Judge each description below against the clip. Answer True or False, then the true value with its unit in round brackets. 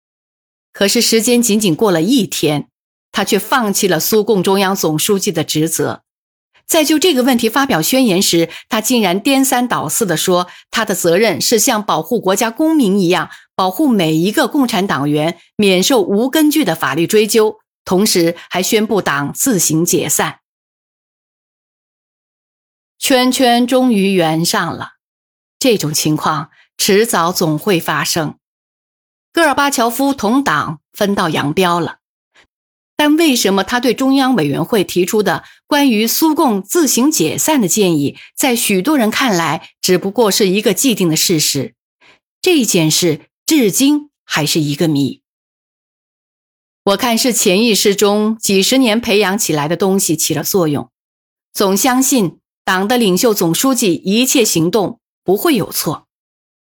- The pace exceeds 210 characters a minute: True (220 characters per minute)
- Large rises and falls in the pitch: True (6.2 semitones)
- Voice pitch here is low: False (205 Hz)